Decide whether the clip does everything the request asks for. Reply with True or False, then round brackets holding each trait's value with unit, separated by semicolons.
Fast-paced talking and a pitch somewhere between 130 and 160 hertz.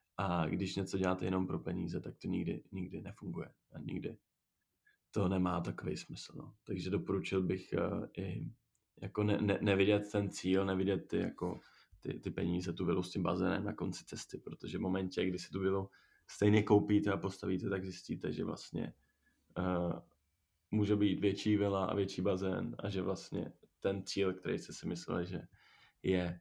False (175 wpm; 95 Hz)